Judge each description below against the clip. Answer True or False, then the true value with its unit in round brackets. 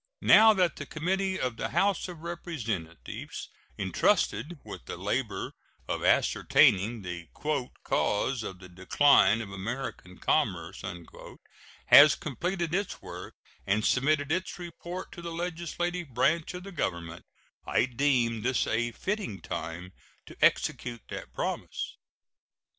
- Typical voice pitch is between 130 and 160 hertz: True (135 Hz)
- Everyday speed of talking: False (125 wpm)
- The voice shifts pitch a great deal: True (8.8 semitones)